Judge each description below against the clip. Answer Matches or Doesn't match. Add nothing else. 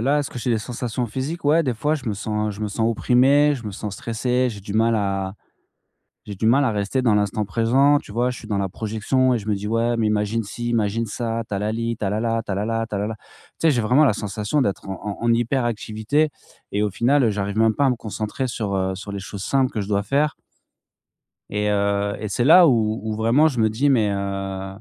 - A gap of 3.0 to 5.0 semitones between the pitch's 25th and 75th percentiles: Matches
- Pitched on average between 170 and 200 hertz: Doesn't match